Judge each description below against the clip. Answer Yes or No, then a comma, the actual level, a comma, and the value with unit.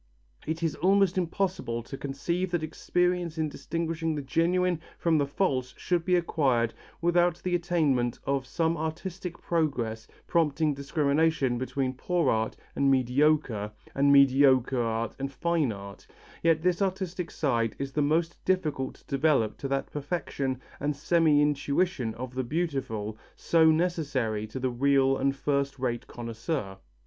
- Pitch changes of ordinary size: Yes, average, 4.4 semitones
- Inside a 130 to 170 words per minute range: Yes, average, 145 wpm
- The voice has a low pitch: No, medium, 145 Hz